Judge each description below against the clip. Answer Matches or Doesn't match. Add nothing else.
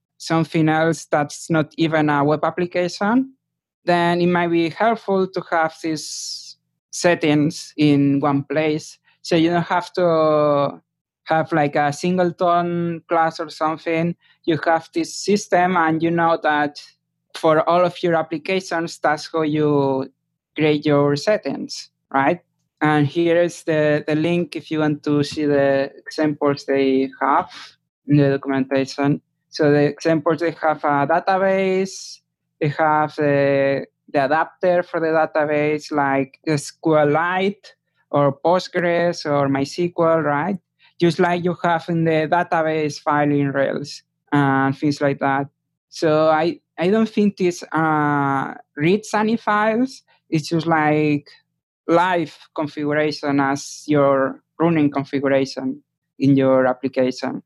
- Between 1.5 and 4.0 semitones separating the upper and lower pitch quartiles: Matches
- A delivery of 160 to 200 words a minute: Doesn't match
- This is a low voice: Doesn't match